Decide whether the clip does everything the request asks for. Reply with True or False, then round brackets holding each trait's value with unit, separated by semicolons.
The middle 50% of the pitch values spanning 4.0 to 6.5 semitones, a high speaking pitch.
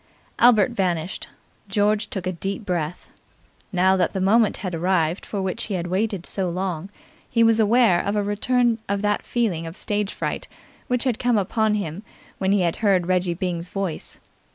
False (3.0 semitones; 195 Hz)